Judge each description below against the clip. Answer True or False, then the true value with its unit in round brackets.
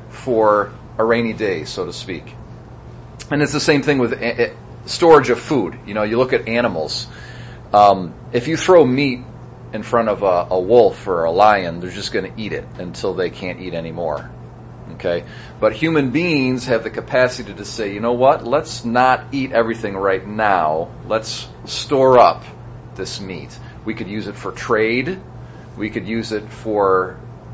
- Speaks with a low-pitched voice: True (120 Hz)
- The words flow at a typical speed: True (175 wpm)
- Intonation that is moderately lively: True (3.2 semitones)